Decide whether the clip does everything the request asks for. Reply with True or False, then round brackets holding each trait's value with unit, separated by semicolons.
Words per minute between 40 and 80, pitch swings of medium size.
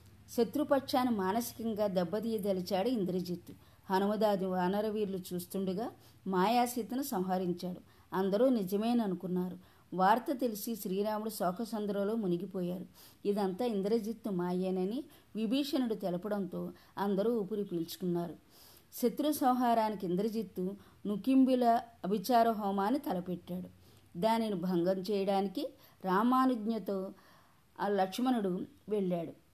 True (75 wpm; 4.0 semitones)